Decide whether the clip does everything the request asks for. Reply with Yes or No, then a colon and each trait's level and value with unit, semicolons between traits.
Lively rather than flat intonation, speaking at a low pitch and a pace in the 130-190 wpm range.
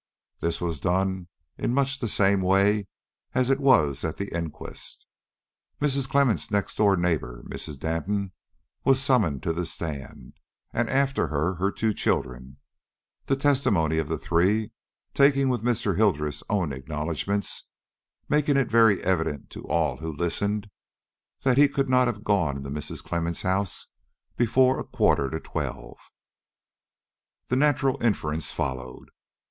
Yes: wide, 7.6 semitones; low, 100 Hz; average, 140 wpm